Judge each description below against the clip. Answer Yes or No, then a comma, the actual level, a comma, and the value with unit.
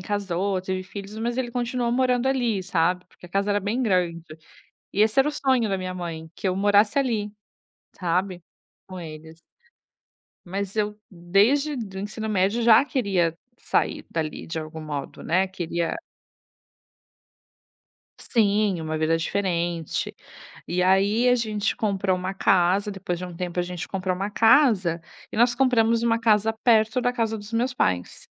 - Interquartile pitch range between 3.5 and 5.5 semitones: Yes, average, 4.1 semitones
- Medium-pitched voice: No, high, 200 Hz